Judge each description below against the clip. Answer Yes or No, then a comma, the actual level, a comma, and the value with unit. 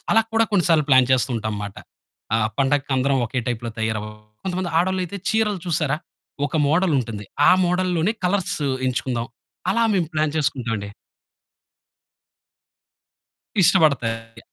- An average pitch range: No, wide, 7.5 semitones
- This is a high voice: No, medium, 145 Hz